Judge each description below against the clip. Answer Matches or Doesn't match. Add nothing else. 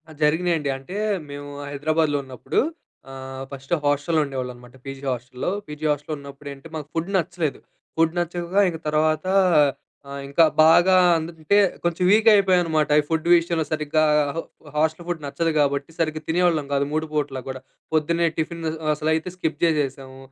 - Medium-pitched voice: Matches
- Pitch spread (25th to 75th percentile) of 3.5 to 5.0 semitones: Doesn't match